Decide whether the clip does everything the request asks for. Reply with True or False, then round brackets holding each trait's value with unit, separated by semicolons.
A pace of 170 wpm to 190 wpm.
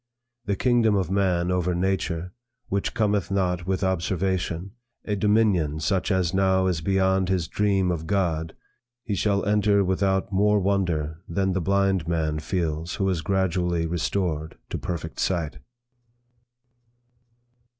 False (135 wpm)